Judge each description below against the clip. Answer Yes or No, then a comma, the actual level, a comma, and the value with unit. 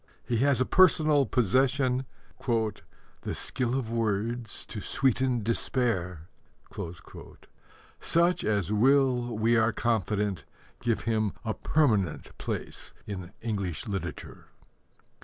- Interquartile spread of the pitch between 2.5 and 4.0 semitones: Yes, average, 3.7 semitones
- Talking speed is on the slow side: Yes, slow, 100 wpm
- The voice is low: Yes, low, 115 Hz